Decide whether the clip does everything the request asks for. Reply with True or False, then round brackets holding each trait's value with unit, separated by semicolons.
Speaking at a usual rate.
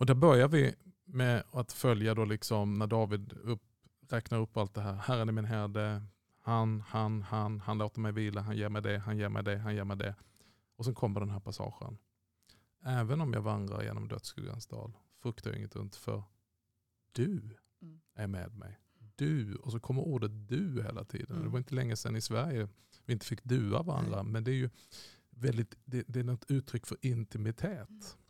False (200 wpm)